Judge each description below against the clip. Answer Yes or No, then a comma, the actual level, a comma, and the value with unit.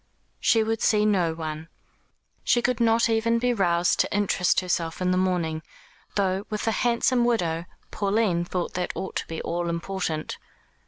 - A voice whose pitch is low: No, high, 190 Hz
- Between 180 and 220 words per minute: No, average, 165 wpm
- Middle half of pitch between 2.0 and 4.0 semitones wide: No, average, 4.7 semitones